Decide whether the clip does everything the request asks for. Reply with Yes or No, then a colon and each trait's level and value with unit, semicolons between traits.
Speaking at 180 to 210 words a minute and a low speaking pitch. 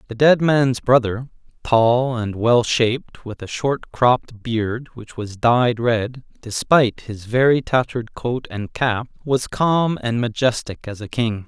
No: average, 160 wpm; low, 120 Hz